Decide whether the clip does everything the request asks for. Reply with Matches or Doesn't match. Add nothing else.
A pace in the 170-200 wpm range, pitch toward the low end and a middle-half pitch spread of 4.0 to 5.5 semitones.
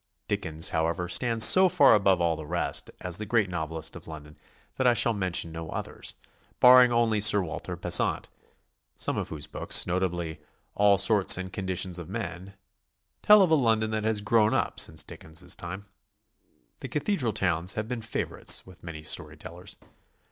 Matches